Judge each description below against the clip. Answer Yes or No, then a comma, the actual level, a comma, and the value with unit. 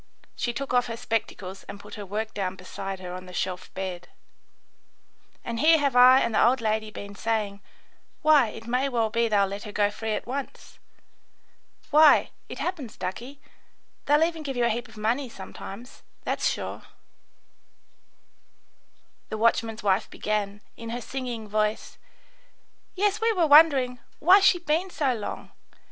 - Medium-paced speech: Yes, average, 160 wpm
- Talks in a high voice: Yes, high, 230 Hz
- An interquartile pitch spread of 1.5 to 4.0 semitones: No, average, 4.5 semitones